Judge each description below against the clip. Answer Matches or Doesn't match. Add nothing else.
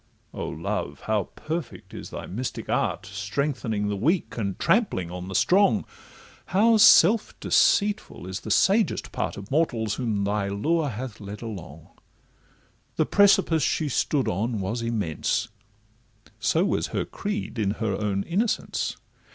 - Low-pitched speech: Matches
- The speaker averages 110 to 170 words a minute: Matches